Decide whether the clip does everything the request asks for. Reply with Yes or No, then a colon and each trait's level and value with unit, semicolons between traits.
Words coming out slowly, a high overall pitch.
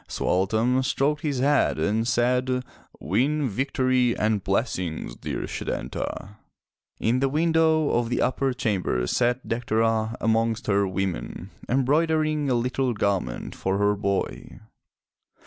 No: slow, 120 wpm; low, 120 Hz